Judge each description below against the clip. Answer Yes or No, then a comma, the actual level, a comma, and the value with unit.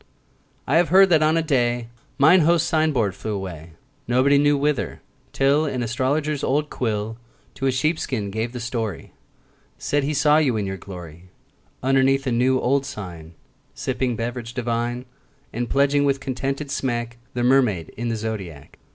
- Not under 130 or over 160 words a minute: No, average, 170 wpm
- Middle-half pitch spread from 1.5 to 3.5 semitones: No, average, 4.0 semitones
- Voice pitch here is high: No, low, 125 Hz